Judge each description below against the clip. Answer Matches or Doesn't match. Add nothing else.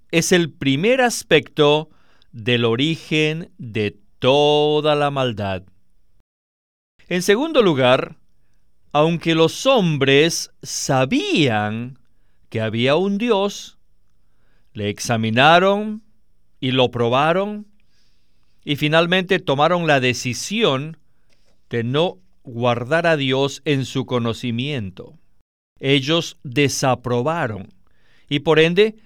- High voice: Doesn't match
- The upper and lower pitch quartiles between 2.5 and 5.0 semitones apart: Doesn't match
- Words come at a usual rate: Doesn't match